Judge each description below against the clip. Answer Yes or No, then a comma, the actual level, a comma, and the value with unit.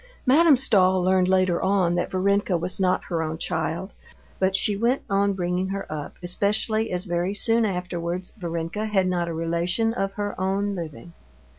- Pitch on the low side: No, medium, 185 Hz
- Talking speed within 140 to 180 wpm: Yes, average, 170 wpm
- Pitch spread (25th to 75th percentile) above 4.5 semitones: No, narrow, 2.5 semitones